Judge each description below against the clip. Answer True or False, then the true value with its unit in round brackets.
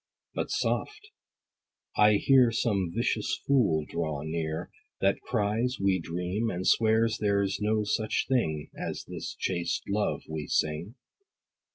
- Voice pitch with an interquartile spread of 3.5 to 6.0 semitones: True (5.2 semitones)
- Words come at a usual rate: False (130 wpm)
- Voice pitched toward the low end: True (100 Hz)